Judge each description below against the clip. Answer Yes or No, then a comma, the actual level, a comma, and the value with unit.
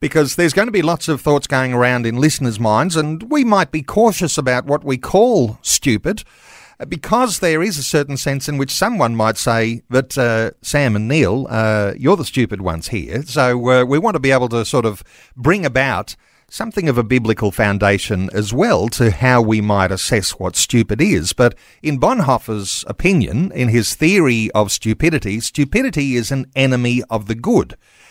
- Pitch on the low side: Yes, low, 125 Hz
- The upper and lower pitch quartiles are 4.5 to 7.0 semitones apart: Yes, average, 5.3 semitones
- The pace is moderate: Yes, average, 190 wpm